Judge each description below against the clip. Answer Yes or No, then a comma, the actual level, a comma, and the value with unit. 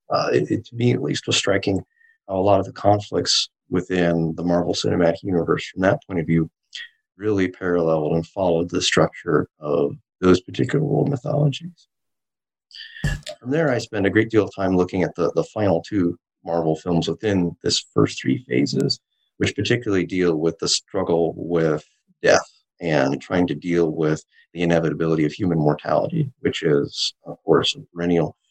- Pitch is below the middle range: Yes, very low, 90 Hz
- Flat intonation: No, average, 4.1 semitones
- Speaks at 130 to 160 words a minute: No, average, 175 wpm